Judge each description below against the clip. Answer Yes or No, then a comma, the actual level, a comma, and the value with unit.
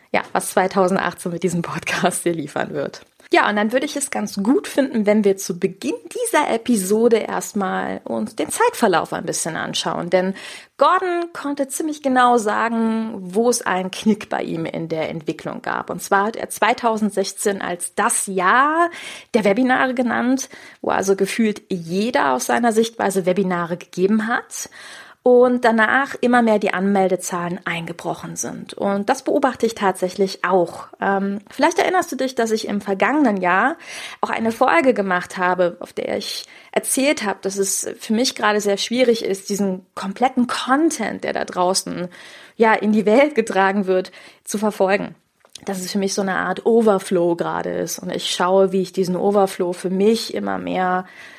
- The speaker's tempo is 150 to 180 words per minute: Yes, average, 170 wpm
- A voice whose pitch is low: No, high, 205 Hz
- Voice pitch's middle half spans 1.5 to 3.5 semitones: No, average, 4.8 semitones